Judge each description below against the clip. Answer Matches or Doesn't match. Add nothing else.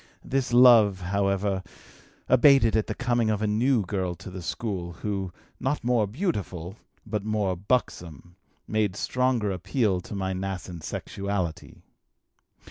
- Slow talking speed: Matches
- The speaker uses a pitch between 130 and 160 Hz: Doesn't match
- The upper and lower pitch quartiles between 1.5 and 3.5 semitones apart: Doesn't match